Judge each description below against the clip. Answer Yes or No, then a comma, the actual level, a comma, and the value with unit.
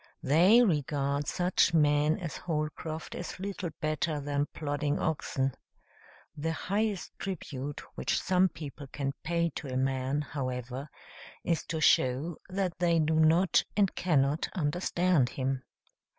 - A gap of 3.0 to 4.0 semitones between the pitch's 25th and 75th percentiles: Yes, average, 3.6 semitones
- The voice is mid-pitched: Yes, medium, 155 Hz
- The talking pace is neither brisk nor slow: No, slow, 130 wpm